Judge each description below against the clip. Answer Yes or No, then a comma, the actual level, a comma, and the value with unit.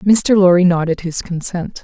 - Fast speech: No, average, 165 wpm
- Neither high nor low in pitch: Yes, medium, 180 Hz